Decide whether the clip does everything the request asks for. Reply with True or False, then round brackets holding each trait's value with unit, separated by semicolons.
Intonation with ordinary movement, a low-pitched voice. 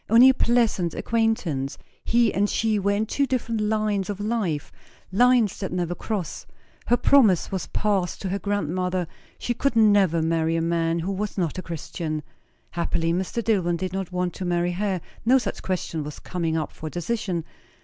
False (4.3 semitones; 190 Hz)